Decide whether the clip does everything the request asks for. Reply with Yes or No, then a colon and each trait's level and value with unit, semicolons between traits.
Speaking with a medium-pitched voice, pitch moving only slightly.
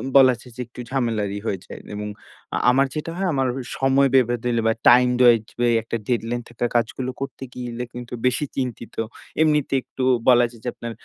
No: low, 125 Hz; narrow, 2.1 semitones